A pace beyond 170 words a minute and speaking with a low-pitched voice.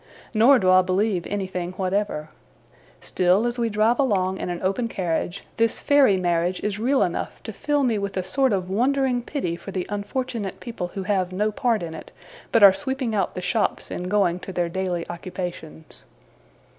No: average, 185 wpm; high, 195 Hz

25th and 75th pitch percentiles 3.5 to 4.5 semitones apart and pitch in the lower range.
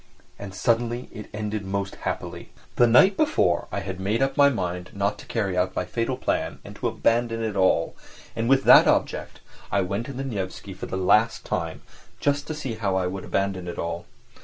Yes: average, 4.1 semitones; low, 105 Hz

